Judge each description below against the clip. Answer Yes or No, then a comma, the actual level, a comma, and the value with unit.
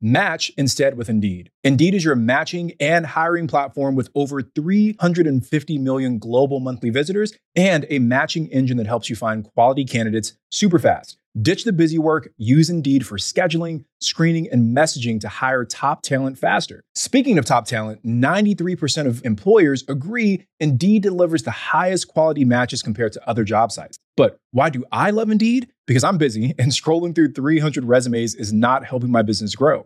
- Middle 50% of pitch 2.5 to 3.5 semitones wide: No, average, 5.3 semitones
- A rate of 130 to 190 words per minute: Yes, average, 170 wpm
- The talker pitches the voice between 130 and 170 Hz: Yes, medium, 140 Hz